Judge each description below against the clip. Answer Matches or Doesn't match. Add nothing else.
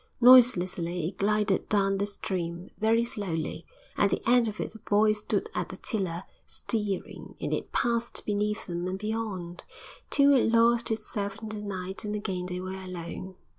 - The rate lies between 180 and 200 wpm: Doesn't match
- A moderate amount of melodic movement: Matches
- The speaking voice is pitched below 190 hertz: Doesn't match